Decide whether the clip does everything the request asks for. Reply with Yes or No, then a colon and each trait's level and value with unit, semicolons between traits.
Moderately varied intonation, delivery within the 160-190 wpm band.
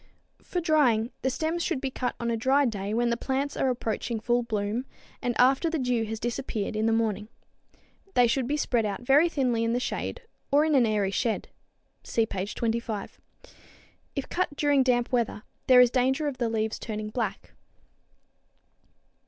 Yes: average, 3.2 semitones; average, 180 wpm